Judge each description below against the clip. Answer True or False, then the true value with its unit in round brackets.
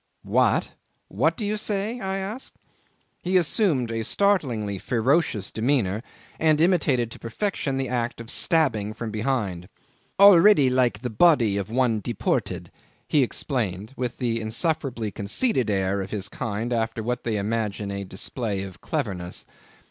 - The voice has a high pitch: False (120 Hz)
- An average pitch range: False (6.5 semitones)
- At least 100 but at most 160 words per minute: True (145 wpm)